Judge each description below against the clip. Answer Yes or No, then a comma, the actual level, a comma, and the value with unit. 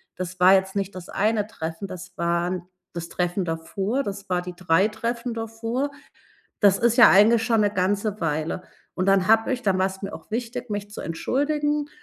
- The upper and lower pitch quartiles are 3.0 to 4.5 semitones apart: Yes, average, 3.8 semitones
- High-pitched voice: Yes, high, 200 Hz